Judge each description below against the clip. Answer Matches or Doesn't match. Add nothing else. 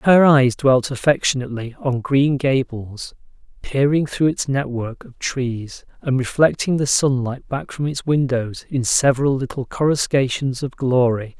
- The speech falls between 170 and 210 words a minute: Doesn't match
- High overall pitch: Doesn't match